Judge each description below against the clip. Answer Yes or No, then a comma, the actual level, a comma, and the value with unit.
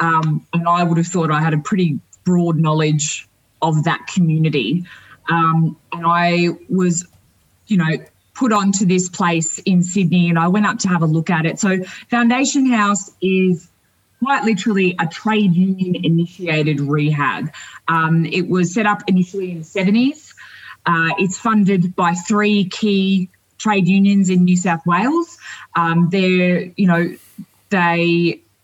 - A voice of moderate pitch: Yes, medium, 175 Hz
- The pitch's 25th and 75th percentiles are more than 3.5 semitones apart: No, average, 3.0 semitones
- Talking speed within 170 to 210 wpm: No, average, 155 wpm